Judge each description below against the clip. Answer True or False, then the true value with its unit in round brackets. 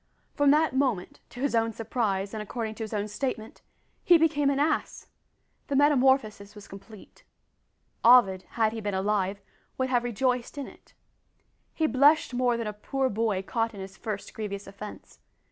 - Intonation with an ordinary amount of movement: True (4.3 semitones)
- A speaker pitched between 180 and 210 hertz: False (225 Hz)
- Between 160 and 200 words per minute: True (170 wpm)